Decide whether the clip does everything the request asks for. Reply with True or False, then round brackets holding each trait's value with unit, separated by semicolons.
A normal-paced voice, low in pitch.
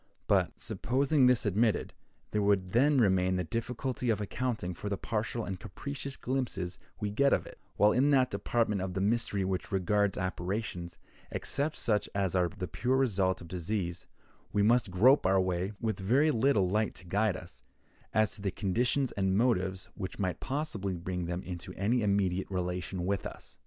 True (175 wpm; 100 Hz)